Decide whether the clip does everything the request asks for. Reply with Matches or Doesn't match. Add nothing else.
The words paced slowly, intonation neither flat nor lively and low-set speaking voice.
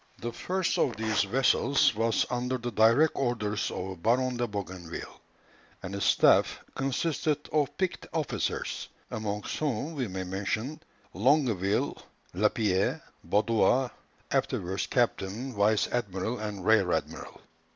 Matches